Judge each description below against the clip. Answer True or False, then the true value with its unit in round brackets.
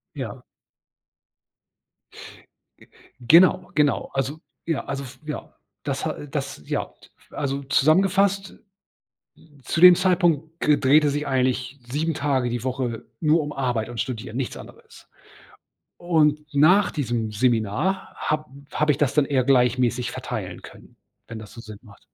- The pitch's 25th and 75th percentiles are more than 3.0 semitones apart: True (4.0 semitones)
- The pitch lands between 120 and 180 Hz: True (140 Hz)